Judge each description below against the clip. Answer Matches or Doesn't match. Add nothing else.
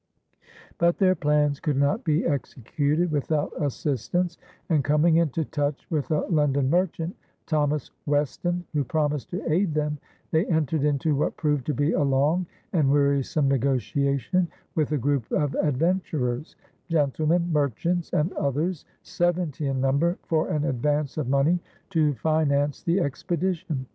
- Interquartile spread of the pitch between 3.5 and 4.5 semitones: Doesn't match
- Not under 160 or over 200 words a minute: Doesn't match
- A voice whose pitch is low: Doesn't match